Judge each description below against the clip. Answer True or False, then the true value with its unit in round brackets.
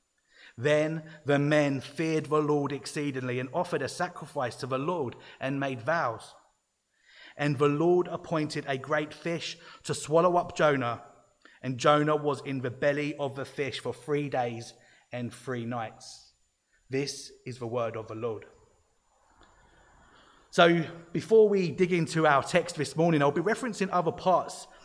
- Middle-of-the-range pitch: True (150 Hz)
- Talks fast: False (155 wpm)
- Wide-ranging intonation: False (3.9 semitones)